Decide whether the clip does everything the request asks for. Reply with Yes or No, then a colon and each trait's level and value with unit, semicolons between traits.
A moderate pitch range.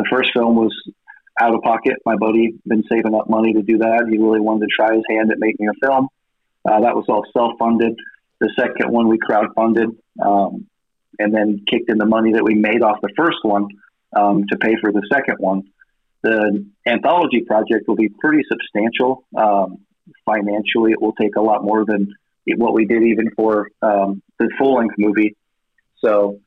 No: narrow, 1.4 semitones